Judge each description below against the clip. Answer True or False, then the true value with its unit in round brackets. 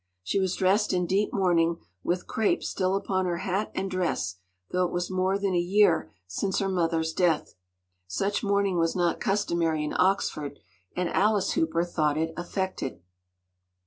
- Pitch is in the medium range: True (180 Hz)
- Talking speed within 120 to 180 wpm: True (165 wpm)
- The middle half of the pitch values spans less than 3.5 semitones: True (2.7 semitones)